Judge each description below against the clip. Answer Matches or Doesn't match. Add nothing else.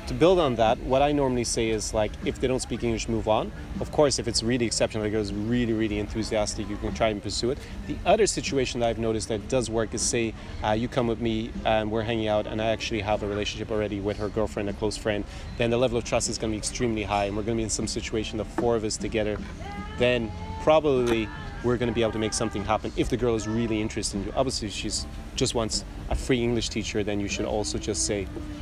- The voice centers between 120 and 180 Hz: Doesn't match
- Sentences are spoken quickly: Matches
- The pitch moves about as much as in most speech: Doesn't match